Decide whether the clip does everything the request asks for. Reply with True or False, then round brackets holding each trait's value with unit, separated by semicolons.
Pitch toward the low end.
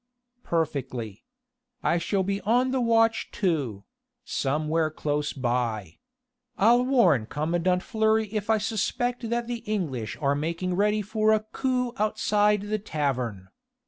False (195 Hz)